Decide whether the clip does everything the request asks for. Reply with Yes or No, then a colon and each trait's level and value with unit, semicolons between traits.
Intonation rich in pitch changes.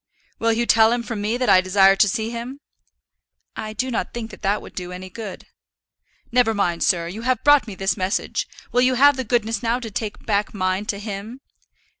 No: average, 3.4 semitones